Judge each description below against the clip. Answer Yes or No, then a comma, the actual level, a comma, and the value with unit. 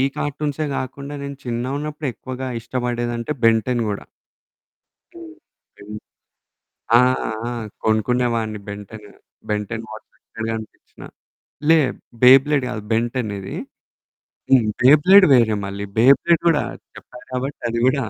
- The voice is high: No, low, 125 Hz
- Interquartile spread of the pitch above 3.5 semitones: Yes, average, 4.0 semitones